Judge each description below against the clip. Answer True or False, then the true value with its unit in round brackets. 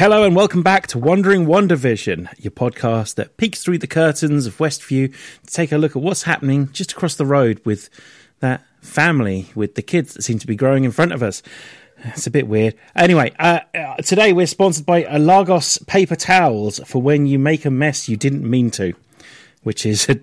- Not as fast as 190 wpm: False (200 wpm)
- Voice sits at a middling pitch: True (145 Hz)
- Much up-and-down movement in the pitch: True (5.9 semitones)